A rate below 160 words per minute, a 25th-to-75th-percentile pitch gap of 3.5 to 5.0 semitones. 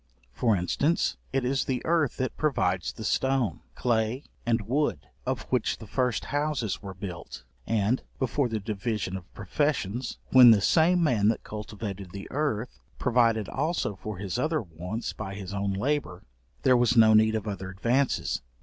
No: average, 165 wpm; average, 4.7 semitones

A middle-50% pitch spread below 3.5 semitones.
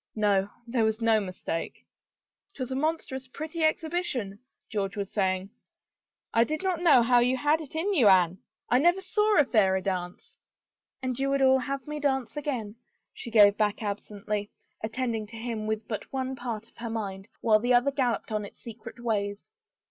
No: average, 4.7 semitones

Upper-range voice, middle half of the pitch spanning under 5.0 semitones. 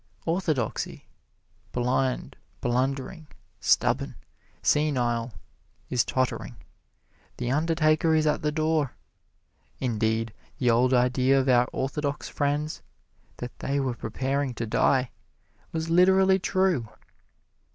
No: low, 135 Hz; average, 3.9 semitones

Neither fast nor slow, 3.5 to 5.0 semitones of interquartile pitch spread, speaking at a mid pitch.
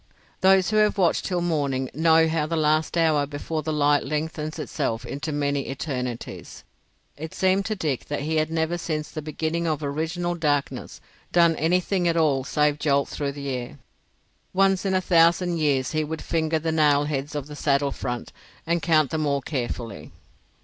No: average, 180 wpm; narrow, 2.6 semitones; medium, 155 Hz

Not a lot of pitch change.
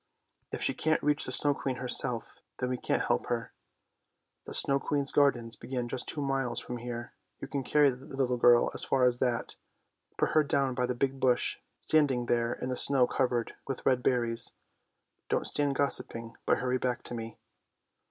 Yes: narrow, 2.1 semitones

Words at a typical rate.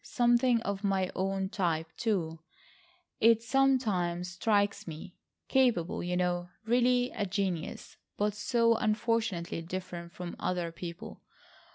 No: slow, 115 wpm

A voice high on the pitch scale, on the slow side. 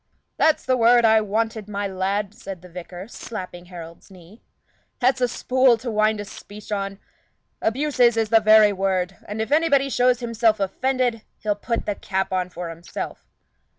No: high, 215 Hz; average, 170 wpm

